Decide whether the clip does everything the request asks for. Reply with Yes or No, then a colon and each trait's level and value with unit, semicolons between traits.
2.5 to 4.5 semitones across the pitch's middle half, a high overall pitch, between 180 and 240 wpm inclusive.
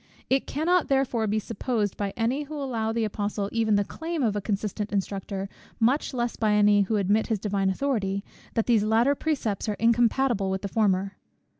Yes: average, 3.2 semitones; high, 220 Hz; average, 190 wpm